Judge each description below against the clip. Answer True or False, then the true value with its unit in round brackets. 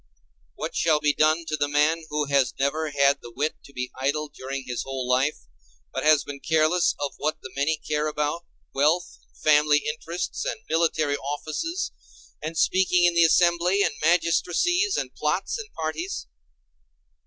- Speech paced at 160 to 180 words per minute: True (165 wpm)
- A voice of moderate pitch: True (155 Hz)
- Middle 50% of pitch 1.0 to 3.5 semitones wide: True (2.8 semitones)